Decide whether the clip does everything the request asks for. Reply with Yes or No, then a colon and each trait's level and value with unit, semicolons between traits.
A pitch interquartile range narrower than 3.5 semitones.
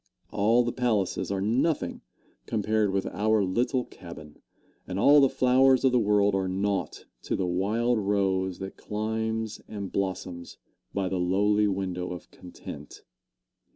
Yes: average, 2.9 semitones